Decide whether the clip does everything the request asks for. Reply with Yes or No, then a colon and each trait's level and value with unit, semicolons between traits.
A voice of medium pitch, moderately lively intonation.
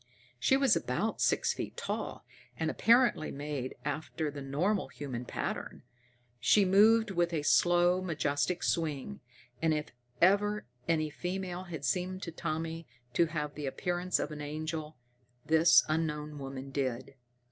Yes: medium, 160 Hz; average, 3.7 semitones